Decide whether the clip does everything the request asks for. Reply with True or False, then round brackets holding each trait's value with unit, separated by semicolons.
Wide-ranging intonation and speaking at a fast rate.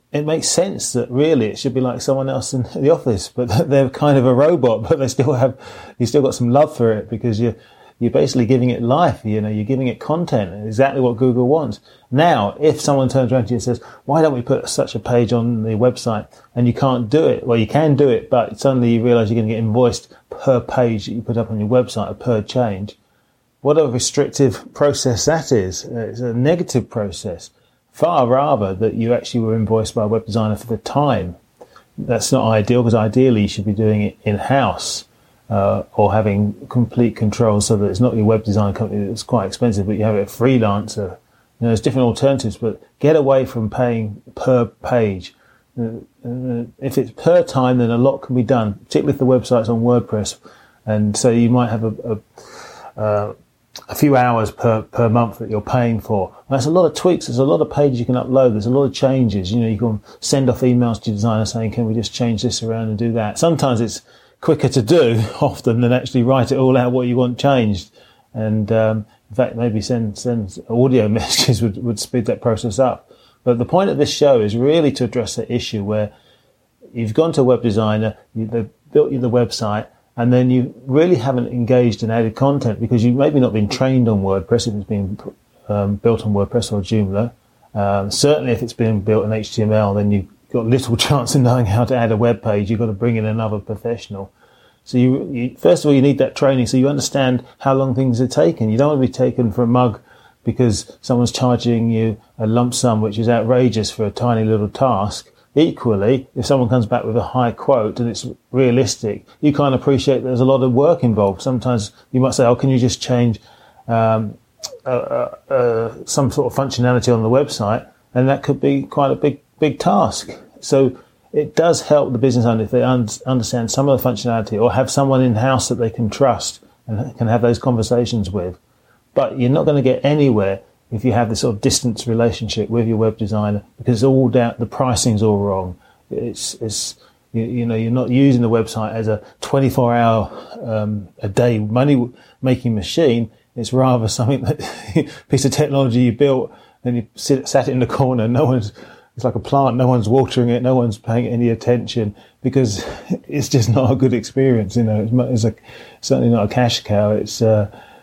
False (2.8 semitones; 215 wpm)